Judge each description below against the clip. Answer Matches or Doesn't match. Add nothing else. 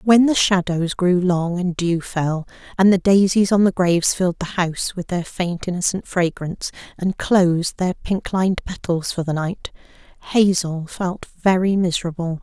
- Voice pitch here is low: Doesn't match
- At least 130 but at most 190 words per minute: Matches